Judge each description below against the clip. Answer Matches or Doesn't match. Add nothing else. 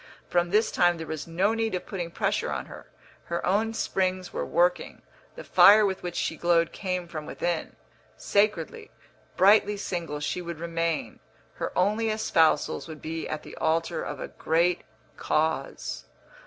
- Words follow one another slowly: Doesn't match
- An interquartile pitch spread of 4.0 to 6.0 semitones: Doesn't match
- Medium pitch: Matches